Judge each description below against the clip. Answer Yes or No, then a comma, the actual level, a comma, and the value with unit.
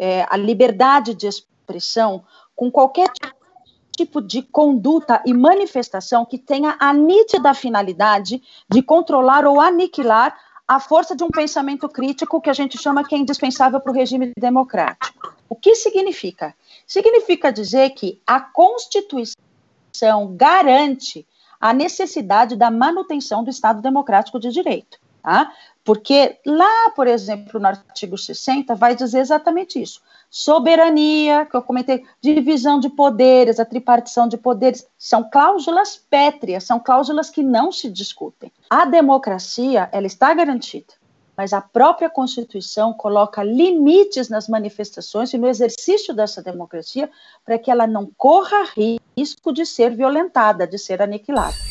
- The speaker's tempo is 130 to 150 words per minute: Yes, average, 135 wpm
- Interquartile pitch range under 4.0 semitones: No, average, 5.2 semitones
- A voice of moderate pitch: No, very high, 260 Hz